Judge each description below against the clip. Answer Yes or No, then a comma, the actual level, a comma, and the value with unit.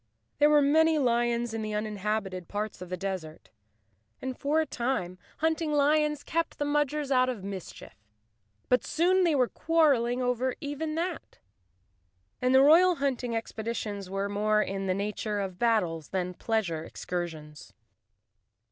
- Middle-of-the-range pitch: No, high, 235 Hz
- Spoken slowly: No, average, 150 wpm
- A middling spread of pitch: No, wide, 6.8 semitones